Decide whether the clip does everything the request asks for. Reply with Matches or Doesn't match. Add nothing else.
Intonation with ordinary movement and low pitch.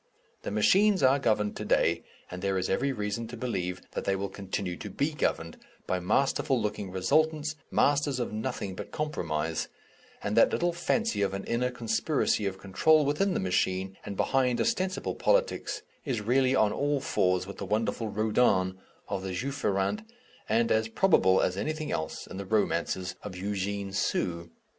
Doesn't match